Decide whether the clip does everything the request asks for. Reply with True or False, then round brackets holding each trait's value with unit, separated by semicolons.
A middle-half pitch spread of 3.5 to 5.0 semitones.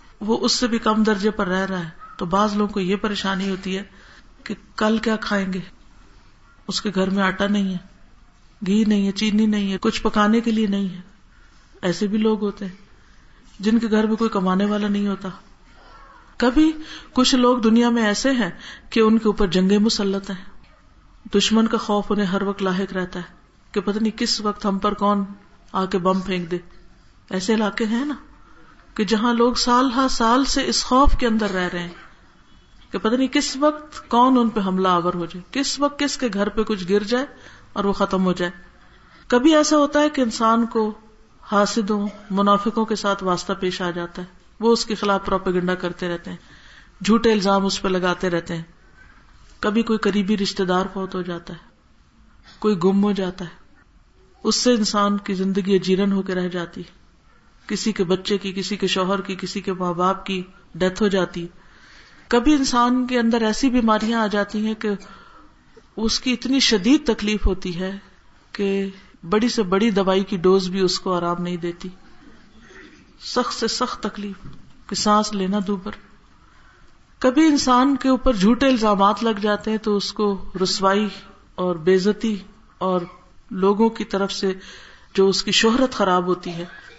False (3.0 semitones)